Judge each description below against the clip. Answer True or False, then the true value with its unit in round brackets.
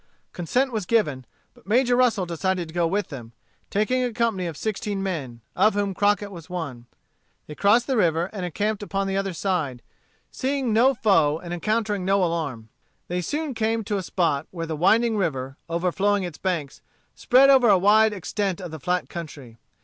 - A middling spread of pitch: True (4.6 semitones)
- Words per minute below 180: False (185 wpm)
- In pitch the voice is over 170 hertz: True (190 Hz)